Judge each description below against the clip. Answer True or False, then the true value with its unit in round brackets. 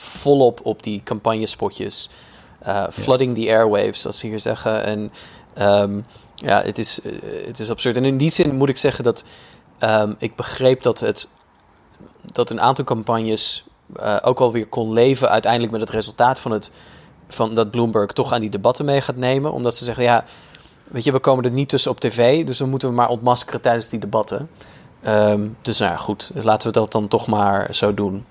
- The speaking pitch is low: True (115 Hz)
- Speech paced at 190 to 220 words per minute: True (195 wpm)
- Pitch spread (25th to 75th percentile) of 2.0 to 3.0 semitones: True (2.7 semitones)